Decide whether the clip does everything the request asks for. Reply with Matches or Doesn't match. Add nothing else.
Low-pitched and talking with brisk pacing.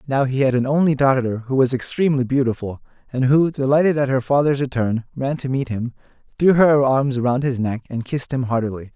Matches